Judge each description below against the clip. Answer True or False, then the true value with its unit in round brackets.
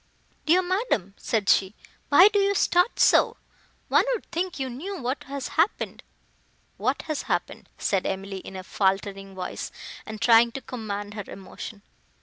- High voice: True (230 Hz)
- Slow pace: False (155 wpm)